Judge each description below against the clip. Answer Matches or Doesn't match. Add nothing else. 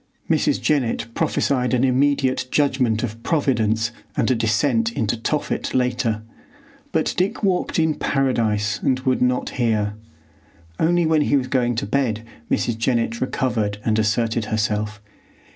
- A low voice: Matches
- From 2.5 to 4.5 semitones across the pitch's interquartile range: Matches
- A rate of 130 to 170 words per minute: Matches